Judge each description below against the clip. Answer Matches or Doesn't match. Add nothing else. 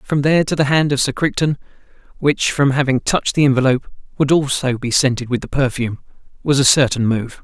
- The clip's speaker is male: Matches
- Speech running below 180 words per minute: Doesn't match